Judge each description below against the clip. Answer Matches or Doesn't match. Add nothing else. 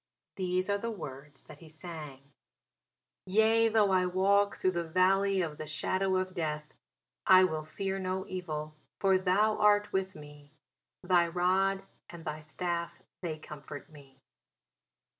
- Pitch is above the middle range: Doesn't match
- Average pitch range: Matches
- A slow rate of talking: Doesn't match